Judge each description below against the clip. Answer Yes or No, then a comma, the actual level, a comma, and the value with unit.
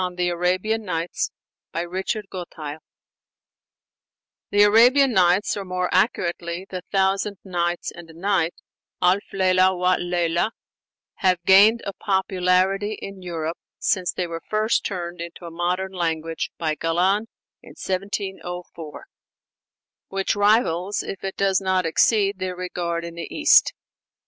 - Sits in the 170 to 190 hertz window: Yes, medium, 185 Hz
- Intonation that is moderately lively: No, narrow, 2.3 semitones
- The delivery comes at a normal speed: No, slow, 130 wpm